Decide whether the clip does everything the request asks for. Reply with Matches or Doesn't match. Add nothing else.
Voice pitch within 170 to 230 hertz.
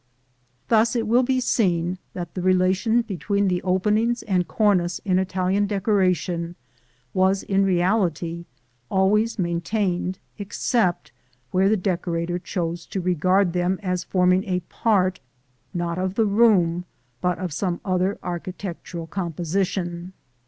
Matches